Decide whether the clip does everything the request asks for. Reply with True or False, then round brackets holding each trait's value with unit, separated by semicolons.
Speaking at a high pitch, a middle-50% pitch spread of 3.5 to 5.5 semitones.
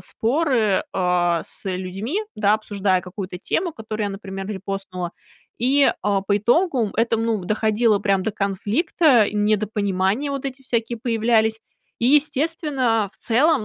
True (215 Hz; 4.0 semitones)